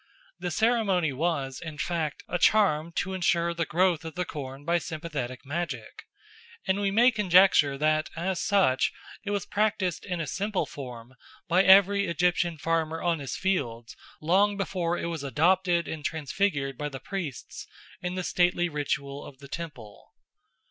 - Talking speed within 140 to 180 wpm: Yes, average, 160 wpm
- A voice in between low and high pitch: Yes, medium, 170 Hz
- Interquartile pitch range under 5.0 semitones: Yes, average, 4.3 semitones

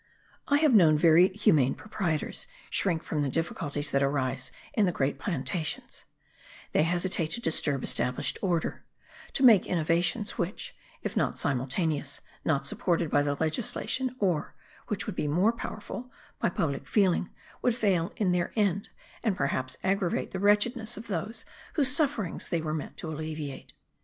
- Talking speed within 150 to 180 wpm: Yes, average, 155 wpm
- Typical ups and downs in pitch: No, wide, 5.7 semitones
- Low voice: No, medium, 170 Hz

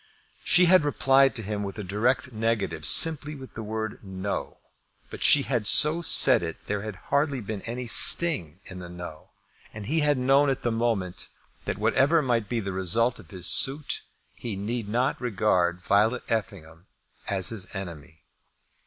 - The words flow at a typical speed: Yes, average, 175 wpm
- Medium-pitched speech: No, low, 110 Hz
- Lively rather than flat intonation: Yes, wide, 5.7 semitones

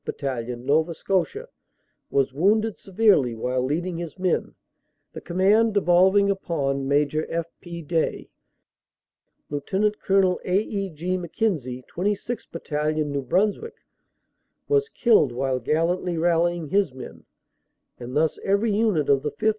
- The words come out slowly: Yes, slow, 130 wpm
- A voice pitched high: No, medium, 170 Hz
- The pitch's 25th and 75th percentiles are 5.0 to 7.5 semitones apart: Yes, wide, 5.6 semitones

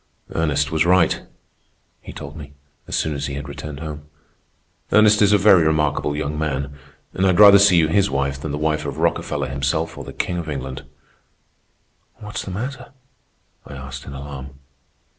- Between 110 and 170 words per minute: No, average, 180 wpm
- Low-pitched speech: Yes, very low, 75 Hz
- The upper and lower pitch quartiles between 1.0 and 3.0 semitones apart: No, average, 3.6 semitones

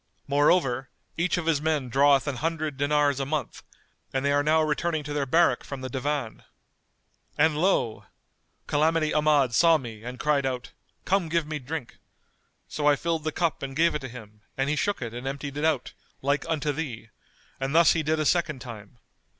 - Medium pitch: Yes, medium, 145 Hz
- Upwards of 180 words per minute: Yes, average, 190 wpm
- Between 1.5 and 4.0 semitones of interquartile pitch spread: Yes, average, 3.0 semitones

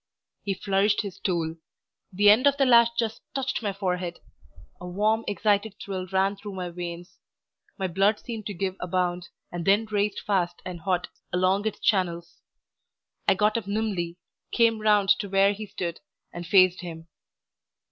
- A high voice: Yes, high, 195 Hz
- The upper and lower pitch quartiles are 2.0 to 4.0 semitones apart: Yes, average, 2.8 semitones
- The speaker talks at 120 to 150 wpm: No, average, 165 wpm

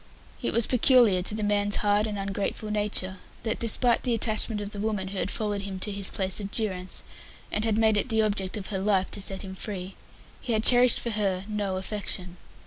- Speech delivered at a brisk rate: Yes, fast, 220 wpm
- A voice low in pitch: No, high, 205 Hz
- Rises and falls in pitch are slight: Yes, narrow, 2.1 semitones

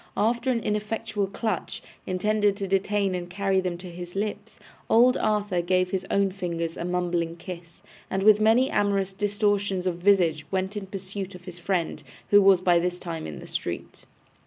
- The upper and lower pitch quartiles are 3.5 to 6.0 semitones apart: No, narrow, 2.5 semitones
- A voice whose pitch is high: Yes, high, 195 Hz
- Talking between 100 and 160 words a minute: No, average, 180 wpm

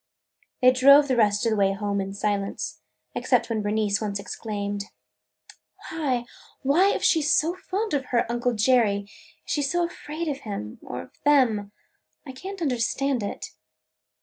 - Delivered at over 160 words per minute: Yes, average, 175 wpm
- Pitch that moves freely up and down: Yes, wide, 5.8 semitones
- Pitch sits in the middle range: No, high, 240 Hz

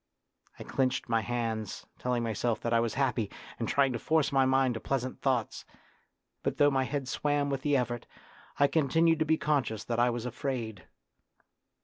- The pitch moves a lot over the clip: No, average, 3.1 semitones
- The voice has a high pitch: No, low, 130 Hz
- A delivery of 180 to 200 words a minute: Yes, average, 185 wpm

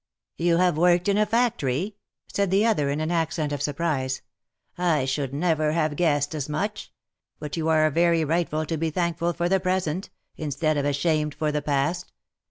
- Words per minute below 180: No, average, 195 wpm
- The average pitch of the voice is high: No, medium, 160 Hz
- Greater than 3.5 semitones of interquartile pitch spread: No, average, 2.9 semitones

